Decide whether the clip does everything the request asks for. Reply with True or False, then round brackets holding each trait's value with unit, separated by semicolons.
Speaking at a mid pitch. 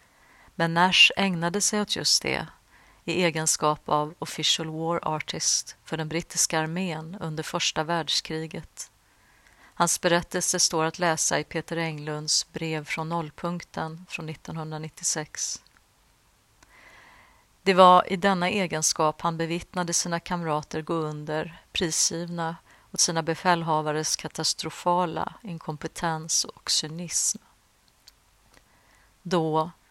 True (165 Hz)